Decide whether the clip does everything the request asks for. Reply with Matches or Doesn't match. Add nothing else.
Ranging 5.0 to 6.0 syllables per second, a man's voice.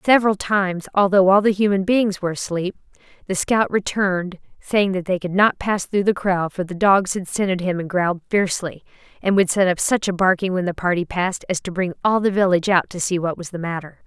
Doesn't match